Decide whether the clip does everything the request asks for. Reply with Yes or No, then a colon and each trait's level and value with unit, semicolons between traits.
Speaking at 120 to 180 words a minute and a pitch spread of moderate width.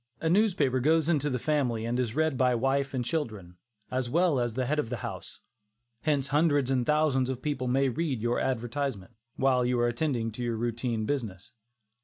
No: average, 195 wpm; average, 3.5 semitones